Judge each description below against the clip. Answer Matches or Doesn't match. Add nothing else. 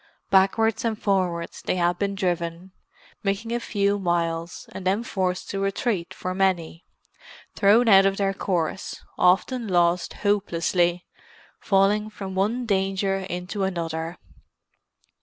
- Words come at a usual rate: Doesn't match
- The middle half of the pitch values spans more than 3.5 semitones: Doesn't match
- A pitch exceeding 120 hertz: Matches